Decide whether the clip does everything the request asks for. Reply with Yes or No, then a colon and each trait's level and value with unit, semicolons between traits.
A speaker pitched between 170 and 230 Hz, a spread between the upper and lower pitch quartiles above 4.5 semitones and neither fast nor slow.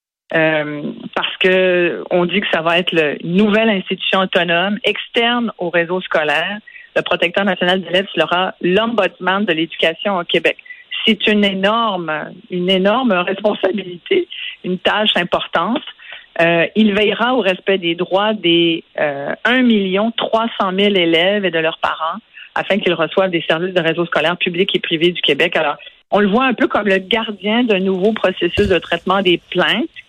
No: high, 190 Hz; average, 3.4 semitones; average, 170 wpm